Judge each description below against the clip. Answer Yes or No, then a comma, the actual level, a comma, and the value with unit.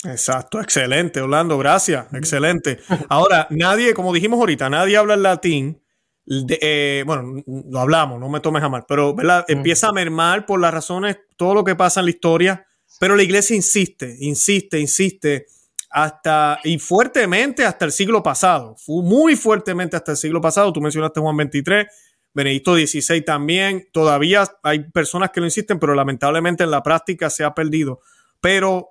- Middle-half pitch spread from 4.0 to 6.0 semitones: Yes, average, 4.3 semitones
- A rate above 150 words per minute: Yes, average, 170 wpm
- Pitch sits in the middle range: Yes, medium, 165 Hz